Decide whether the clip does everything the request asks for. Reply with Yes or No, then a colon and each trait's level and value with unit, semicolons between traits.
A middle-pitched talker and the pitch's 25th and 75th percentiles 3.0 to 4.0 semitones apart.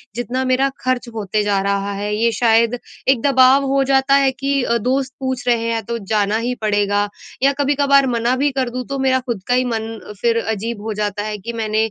No: high, 240 Hz; average, 3.4 semitones